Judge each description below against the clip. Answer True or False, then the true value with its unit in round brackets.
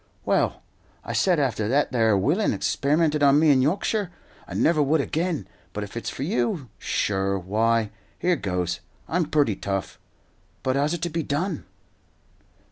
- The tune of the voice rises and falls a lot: True (6.6 semitones)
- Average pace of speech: True (160 wpm)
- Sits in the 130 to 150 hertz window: True (140 Hz)